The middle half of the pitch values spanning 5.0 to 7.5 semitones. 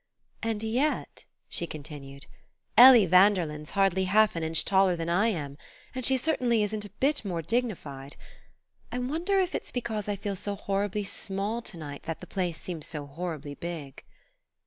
Yes: wide, 5.4 semitones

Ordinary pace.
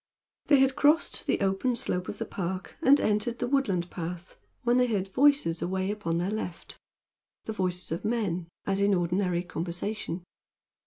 Yes: average, 165 wpm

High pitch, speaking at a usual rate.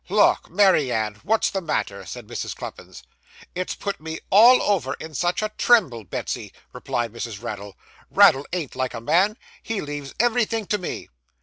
No: medium, 165 Hz; average, 170 wpm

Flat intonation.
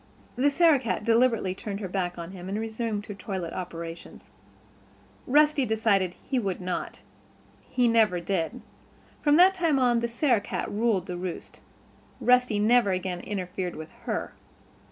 No: average, 5.0 semitones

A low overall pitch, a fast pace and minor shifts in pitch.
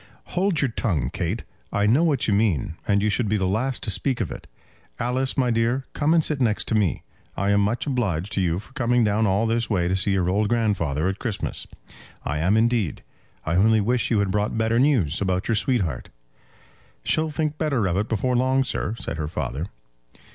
No: low, 110 Hz; fast, 210 wpm; average, 4.5 semitones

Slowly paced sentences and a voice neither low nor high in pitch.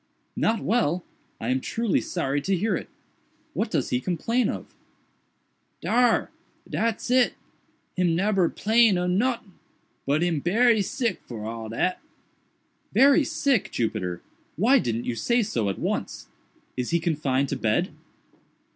Yes: slow, 130 wpm; medium, 180 Hz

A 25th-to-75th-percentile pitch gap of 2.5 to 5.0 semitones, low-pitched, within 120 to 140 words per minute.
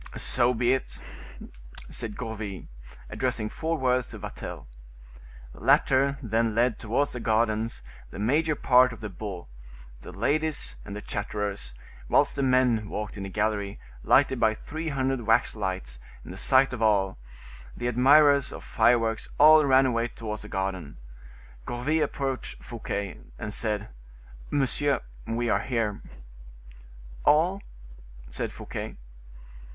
Yes: average, 4.0 semitones; low, 115 Hz; slow, 135 wpm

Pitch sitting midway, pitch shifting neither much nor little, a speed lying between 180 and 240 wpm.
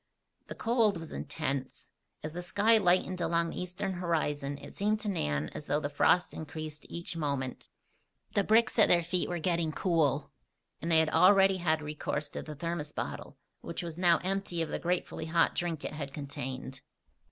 Yes: medium, 165 Hz; average, 3.4 semitones; average, 185 wpm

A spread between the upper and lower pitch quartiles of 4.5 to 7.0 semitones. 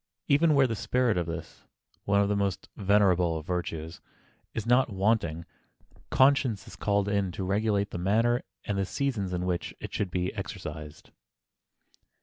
No: average, 4.0 semitones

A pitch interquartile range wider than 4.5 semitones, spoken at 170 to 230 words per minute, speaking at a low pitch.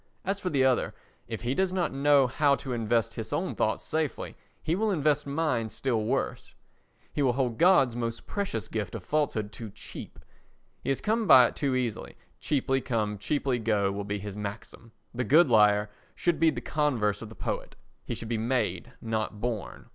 Yes: average, 5.1 semitones; average, 190 wpm; low, 125 Hz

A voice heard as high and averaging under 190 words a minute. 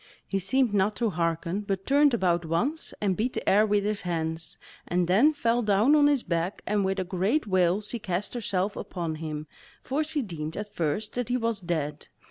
No: high, 200 Hz; fast, 205 wpm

